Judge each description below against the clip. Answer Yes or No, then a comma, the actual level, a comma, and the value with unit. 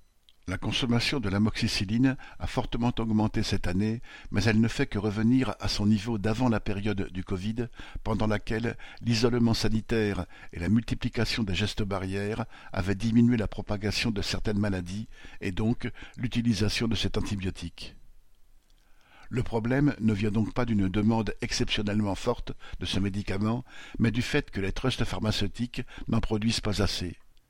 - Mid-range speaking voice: No, low, 110 Hz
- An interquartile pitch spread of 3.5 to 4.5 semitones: No, average, 2.9 semitones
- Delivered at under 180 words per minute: Yes, average, 155 wpm